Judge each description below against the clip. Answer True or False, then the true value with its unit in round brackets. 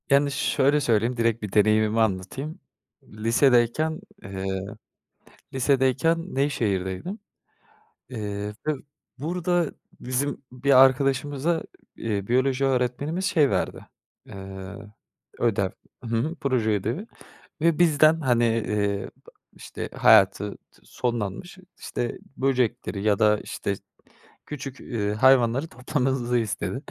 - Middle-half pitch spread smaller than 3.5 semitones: False (4.9 semitones)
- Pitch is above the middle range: False (125 Hz)